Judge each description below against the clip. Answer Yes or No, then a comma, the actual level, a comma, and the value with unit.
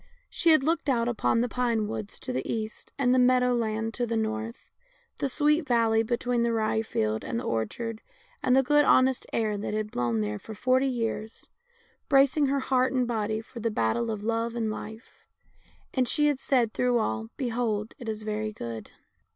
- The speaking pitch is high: Yes, high, 230 Hz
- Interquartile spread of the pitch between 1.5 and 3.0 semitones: Yes, average, 2.7 semitones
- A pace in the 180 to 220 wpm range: Yes, average, 195 wpm